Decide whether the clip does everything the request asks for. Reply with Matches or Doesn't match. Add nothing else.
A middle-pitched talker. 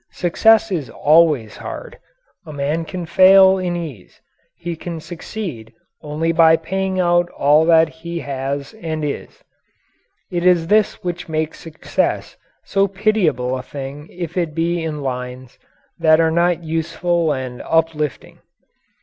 Matches